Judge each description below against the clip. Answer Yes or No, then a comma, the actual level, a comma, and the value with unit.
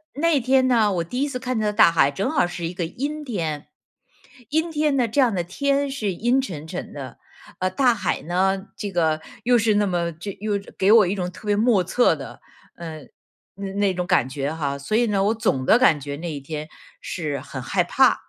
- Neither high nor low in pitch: No, high, 195 Hz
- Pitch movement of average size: No, wide, 6.7 semitones